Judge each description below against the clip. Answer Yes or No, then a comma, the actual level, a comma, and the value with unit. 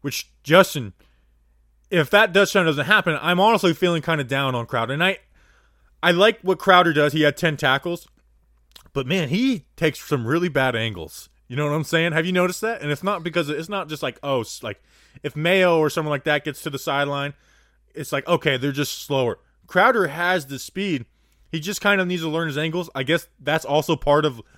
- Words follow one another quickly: Yes, fast, 220 wpm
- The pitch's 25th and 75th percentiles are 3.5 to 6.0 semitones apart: Yes, average, 4.2 semitones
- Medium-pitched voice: Yes, medium, 155 Hz